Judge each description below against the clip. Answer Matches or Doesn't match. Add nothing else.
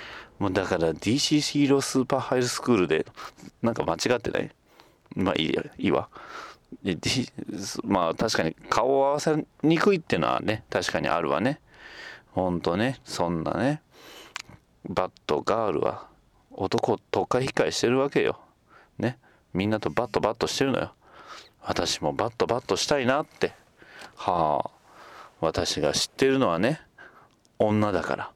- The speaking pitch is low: Matches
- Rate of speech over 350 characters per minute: Doesn't match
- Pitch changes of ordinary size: Doesn't match